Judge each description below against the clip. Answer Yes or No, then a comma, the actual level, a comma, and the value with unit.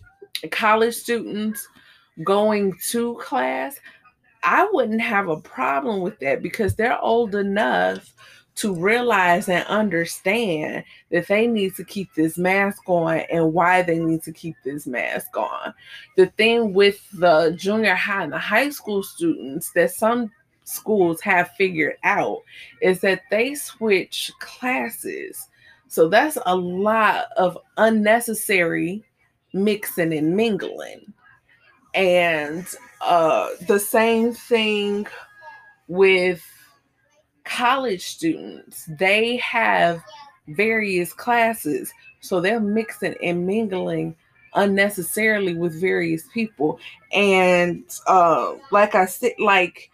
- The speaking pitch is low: No, high, 200 Hz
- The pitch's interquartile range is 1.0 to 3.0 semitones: No, average, 4.5 semitones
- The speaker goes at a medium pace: No, slow, 115 wpm